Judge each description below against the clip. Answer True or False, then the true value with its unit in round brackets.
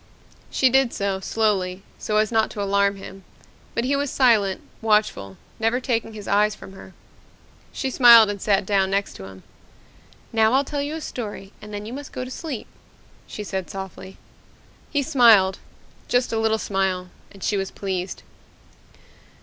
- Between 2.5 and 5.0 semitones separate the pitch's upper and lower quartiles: True (3.6 semitones)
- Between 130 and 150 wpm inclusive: False (170 wpm)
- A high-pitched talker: True (210 Hz)